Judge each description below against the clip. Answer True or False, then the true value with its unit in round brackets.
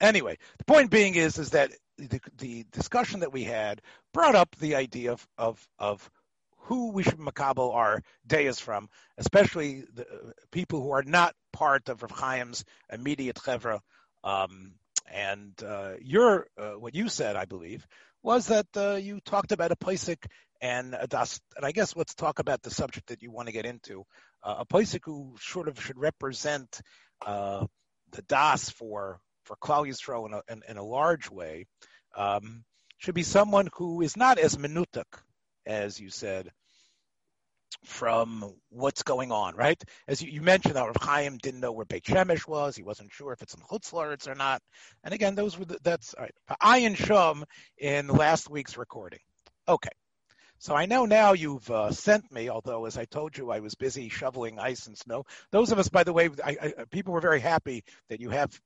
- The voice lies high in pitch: False (140 Hz)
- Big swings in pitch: True (7.3 semitones)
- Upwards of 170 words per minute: True (190 wpm)